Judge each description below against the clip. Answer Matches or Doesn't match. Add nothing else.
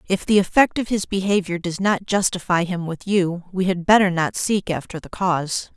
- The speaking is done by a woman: Matches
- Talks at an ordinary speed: Doesn't match